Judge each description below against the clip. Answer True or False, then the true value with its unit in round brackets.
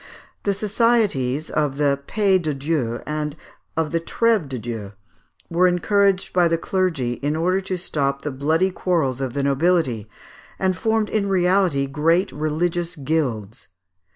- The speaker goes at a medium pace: True (150 wpm)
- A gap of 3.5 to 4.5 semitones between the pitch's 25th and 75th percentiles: False (5.2 semitones)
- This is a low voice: False (160 Hz)